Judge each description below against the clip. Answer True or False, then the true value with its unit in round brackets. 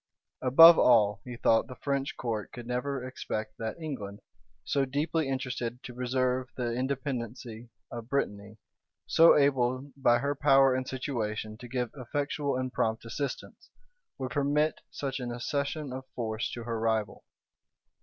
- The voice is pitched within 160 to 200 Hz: False (125 Hz)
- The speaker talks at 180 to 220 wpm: False (145 wpm)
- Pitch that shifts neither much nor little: True (3.0 semitones)